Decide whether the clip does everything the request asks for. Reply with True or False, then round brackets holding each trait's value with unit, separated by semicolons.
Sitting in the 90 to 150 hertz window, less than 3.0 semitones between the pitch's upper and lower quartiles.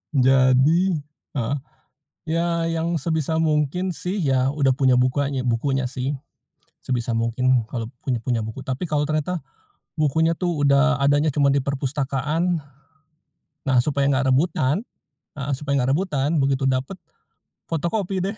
False (140 Hz; 3.7 semitones)